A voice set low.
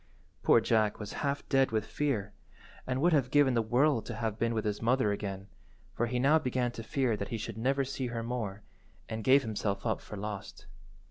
Yes: low, 115 Hz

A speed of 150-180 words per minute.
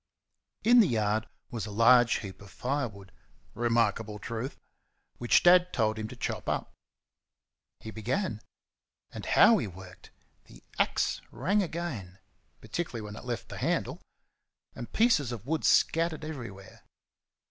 No: slow, 135 wpm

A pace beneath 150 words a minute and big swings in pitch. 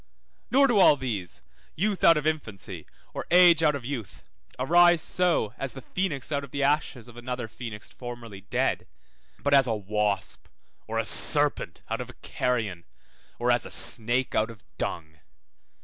No: average, 170 wpm; wide, 5.7 semitones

